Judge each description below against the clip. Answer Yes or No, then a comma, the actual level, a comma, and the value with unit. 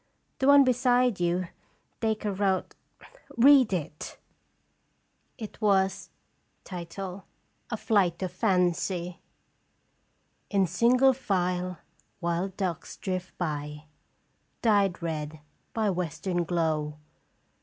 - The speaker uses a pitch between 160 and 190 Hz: Yes, medium, 185 Hz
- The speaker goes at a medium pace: No, slow, 90 wpm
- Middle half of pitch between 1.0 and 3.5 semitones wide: No, average, 3.9 semitones